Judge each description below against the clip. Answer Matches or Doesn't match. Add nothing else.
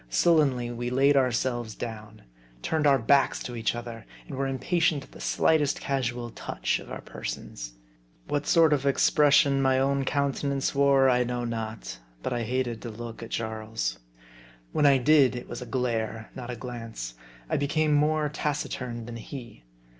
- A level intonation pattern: Doesn't match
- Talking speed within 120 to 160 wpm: Doesn't match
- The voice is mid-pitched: Doesn't match